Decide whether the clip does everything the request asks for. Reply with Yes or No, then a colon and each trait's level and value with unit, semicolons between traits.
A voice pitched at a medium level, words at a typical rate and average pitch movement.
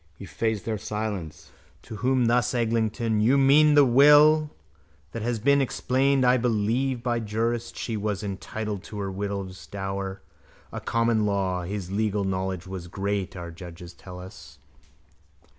No: low, 110 Hz; average, 155 wpm; average, 3.9 semitones